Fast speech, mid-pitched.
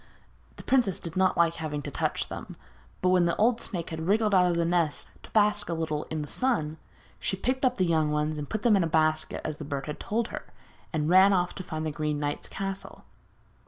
Yes: fast, 235 wpm; medium, 170 Hz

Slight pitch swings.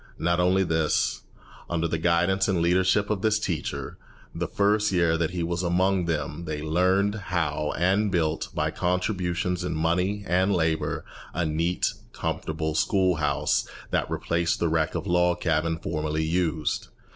Yes: narrow, 2.3 semitones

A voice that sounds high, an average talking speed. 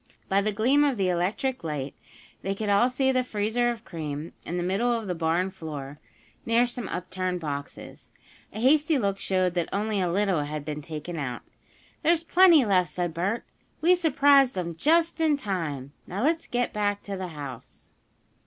Yes: high, 195 Hz; average, 180 wpm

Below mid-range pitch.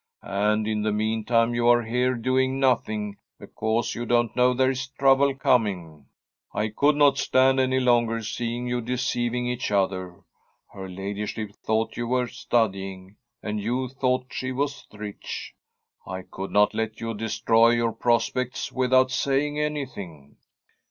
Yes: low, 120 Hz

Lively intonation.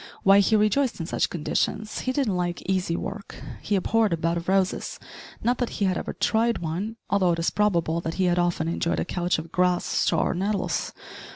No: average, 3.5 semitones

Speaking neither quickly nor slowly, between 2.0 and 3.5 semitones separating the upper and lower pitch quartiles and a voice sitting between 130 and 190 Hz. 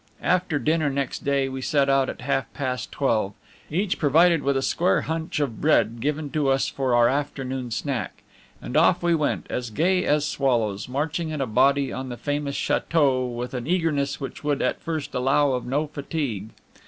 Yes: average, 190 wpm; average, 2.8 semitones; medium, 140 Hz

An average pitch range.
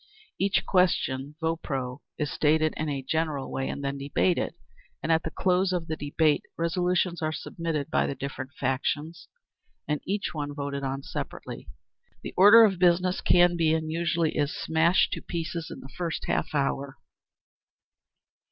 Yes: average, 3.4 semitones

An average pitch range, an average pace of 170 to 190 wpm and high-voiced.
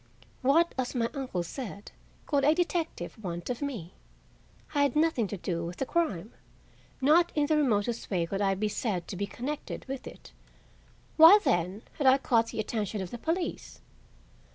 No: wide, 6.9 semitones; average, 175 wpm; high, 240 Hz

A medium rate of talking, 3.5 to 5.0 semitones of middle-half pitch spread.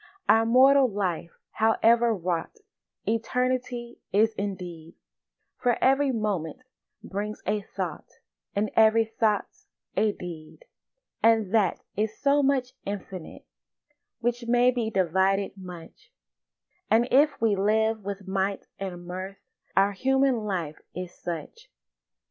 No: slow, 115 wpm; average, 3.9 semitones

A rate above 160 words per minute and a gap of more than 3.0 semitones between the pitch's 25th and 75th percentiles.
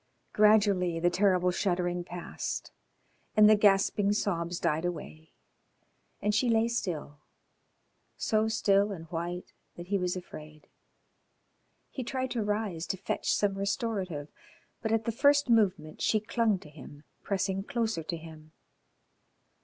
No: slow, 135 wpm; average, 3.9 semitones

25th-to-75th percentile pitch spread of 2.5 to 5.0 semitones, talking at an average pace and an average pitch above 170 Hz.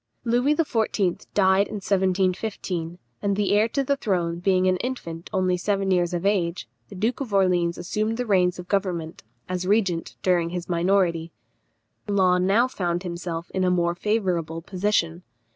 Yes: average, 2.9 semitones; average, 160 wpm; medium, 185 Hz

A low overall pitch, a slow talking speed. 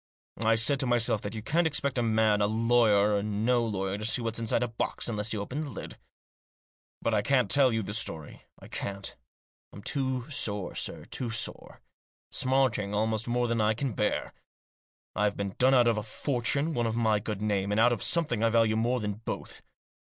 No: low, 115 Hz; average, 200 wpm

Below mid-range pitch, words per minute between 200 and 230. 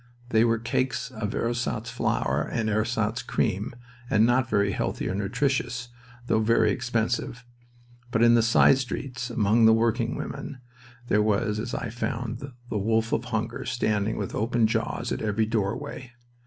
No: low, 115 Hz; average, 155 wpm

